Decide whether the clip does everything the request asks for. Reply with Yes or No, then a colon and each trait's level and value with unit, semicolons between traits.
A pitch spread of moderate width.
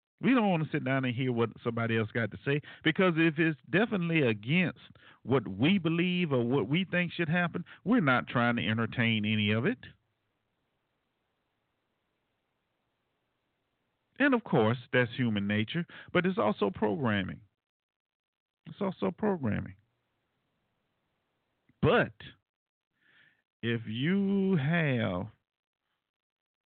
No: wide, 7.3 semitones